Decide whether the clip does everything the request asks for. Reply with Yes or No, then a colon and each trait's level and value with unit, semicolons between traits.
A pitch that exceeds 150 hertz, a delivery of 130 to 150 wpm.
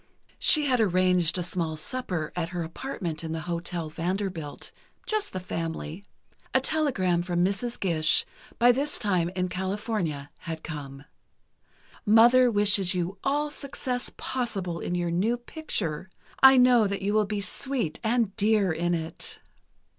Yes: high, 190 Hz; average, 145 wpm